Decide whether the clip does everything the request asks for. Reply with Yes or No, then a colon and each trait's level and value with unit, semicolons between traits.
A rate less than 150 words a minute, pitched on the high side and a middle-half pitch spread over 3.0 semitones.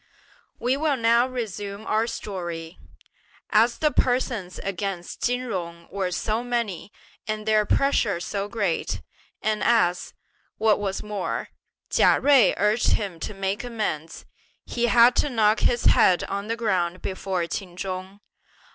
Yes: average, 140 wpm; high, 210 Hz; average, 3.9 semitones